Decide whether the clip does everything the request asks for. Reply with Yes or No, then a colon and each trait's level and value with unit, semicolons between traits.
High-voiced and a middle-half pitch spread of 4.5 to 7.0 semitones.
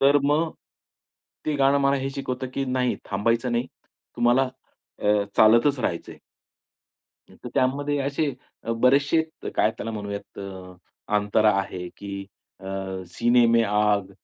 No: low, 120 Hz; average, 5.0 semitones